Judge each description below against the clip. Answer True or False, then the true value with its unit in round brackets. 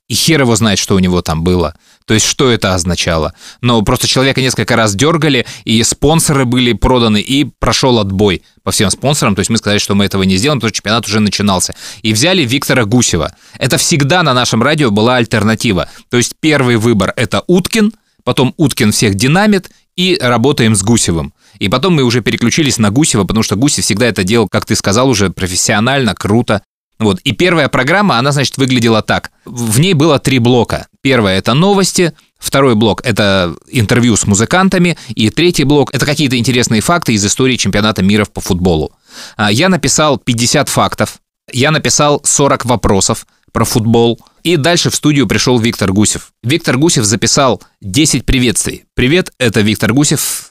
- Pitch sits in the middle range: False (120 Hz)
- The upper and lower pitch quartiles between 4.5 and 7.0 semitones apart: True (5.0 semitones)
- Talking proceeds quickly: True (175 wpm)